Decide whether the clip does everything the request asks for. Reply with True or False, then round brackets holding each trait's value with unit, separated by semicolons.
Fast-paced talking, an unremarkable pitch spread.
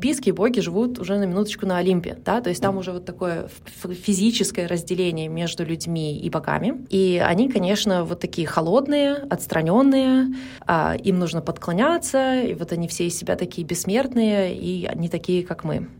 True (175 wpm; 4.6 semitones)